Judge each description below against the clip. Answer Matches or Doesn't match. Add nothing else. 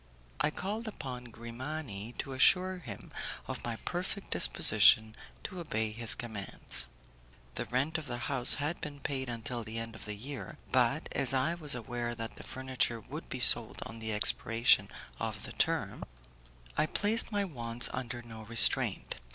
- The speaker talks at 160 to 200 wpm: Matches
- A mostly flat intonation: Doesn't match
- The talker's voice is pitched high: Doesn't match